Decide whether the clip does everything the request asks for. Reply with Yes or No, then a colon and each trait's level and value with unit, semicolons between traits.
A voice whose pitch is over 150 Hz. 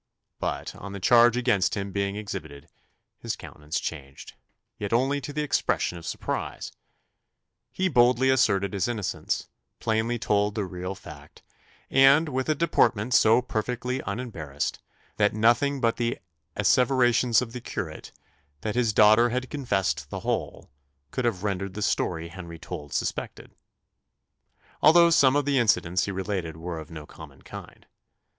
No: low, 110 Hz